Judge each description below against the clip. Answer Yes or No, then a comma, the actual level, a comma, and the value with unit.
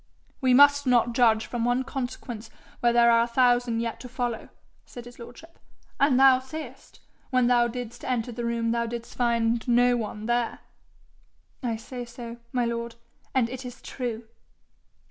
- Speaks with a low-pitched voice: No, high, 240 Hz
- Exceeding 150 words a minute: Yes, average, 170 wpm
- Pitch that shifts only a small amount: Yes, narrow, 1.3 semitones